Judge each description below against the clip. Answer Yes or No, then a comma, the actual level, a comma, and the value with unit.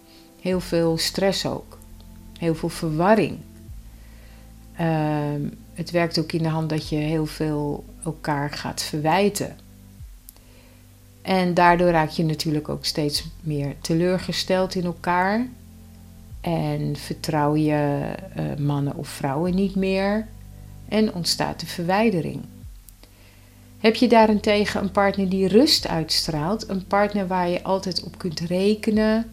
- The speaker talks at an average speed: No, slow, 125 wpm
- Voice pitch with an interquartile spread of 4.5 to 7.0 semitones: Yes, average, 5.3 semitones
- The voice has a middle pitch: Yes, medium, 160 Hz